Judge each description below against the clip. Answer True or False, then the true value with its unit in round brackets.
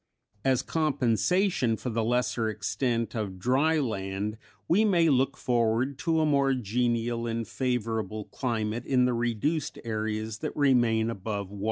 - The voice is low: True (120 Hz)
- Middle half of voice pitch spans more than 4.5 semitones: False (3.5 semitones)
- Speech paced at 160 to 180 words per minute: False (145 wpm)